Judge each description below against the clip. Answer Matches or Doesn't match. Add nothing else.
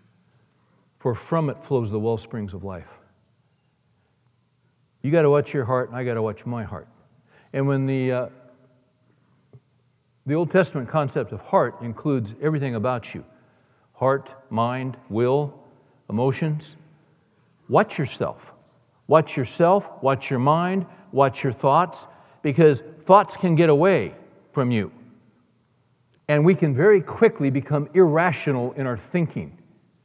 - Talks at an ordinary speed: Doesn't match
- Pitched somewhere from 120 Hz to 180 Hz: Matches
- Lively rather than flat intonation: Doesn't match